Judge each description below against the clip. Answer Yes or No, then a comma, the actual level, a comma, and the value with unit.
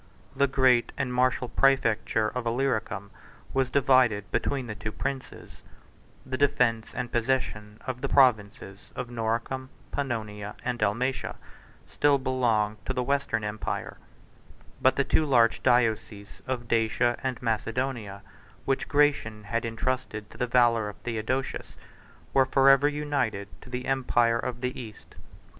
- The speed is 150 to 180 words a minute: No, slow, 135 wpm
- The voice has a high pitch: No, low, 120 Hz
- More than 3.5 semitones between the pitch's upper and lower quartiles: No, average, 3.0 semitones